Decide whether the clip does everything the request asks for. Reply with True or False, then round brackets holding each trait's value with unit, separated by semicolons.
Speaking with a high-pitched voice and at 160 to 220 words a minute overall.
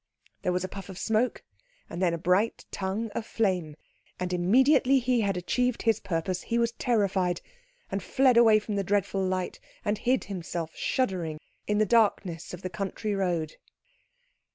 True (195 Hz; 170 wpm)